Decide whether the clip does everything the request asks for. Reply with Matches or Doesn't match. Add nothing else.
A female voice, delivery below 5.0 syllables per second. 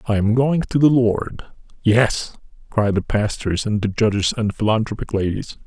Doesn't match